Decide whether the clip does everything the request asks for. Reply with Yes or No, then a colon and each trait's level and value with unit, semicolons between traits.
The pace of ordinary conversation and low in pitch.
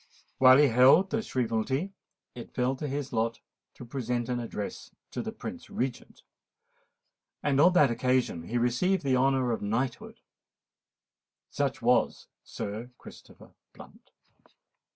No: slow, 130 wpm; low, 125 Hz